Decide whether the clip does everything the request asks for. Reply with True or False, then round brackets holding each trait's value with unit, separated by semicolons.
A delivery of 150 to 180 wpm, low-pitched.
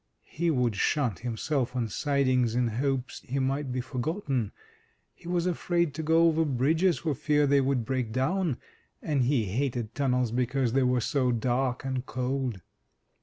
True (165 wpm; 130 Hz)